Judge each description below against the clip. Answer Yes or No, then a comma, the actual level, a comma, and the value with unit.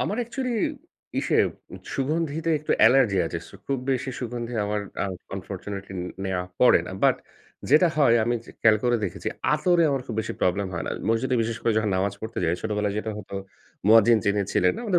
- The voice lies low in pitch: Yes, low, 115 Hz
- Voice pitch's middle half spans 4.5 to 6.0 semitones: Yes, average, 5.2 semitones